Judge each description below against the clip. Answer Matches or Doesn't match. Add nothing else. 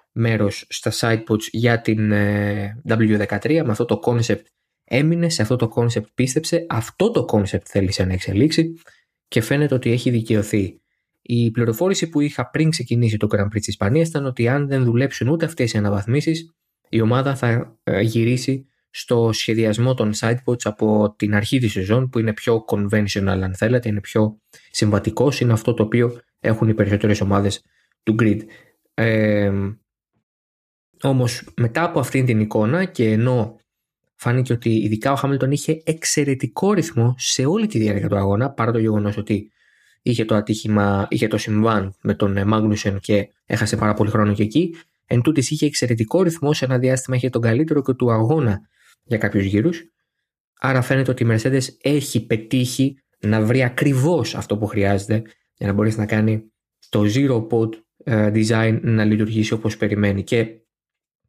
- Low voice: Matches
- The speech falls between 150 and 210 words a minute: Matches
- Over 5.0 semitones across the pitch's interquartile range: Doesn't match